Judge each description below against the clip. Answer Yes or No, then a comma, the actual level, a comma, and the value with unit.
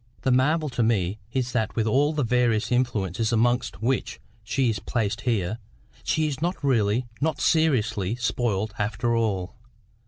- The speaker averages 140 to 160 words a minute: Yes, average, 155 wpm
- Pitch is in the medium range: No, low, 120 Hz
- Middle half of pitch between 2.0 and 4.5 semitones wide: Yes, average, 3.3 semitones